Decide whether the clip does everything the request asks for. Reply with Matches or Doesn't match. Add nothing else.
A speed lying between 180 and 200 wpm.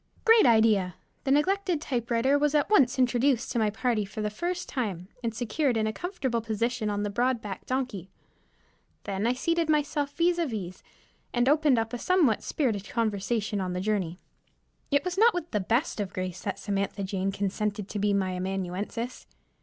Matches